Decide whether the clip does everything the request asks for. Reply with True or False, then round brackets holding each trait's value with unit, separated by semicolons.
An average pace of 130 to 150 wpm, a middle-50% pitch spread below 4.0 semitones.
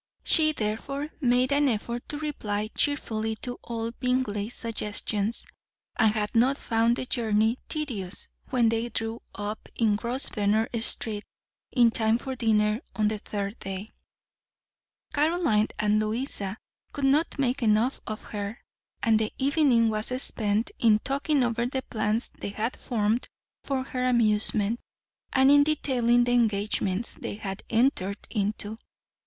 True (140 wpm; 3.3 semitones)